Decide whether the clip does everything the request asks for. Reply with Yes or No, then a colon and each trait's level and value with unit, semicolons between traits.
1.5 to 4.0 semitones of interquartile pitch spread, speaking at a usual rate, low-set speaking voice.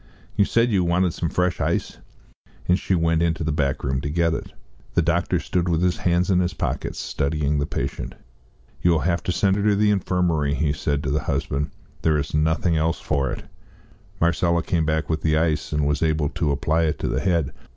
No: average, 2.9 semitones; fast, 215 wpm; very low, 80 Hz